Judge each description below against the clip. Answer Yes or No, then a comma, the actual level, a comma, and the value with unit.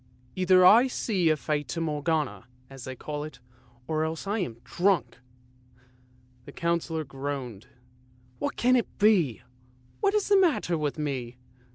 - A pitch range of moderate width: No, wide, 6.4 semitones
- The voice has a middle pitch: Yes, medium, 150 Hz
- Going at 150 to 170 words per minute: Yes, average, 160 wpm